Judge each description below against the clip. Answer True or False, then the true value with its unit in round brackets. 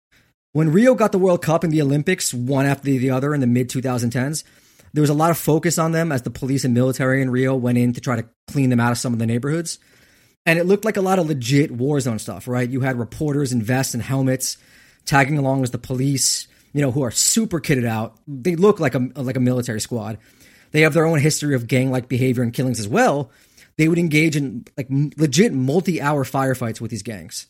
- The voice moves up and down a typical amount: True (3.7 semitones)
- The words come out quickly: True (240 wpm)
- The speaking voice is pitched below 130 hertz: False (135 Hz)